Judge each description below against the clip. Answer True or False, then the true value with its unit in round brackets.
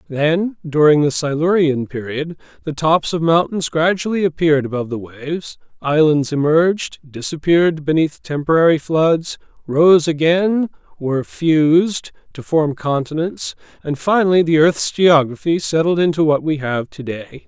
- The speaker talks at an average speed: False (130 wpm)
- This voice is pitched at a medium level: True (155 Hz)